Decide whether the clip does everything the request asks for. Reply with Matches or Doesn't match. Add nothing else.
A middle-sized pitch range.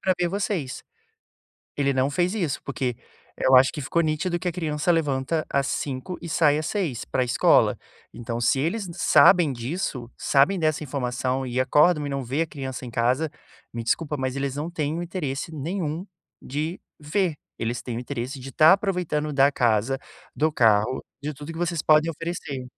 Matches